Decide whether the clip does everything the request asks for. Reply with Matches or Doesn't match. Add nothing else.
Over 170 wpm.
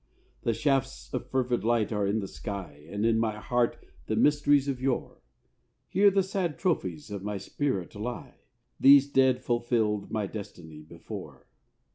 Doesn't match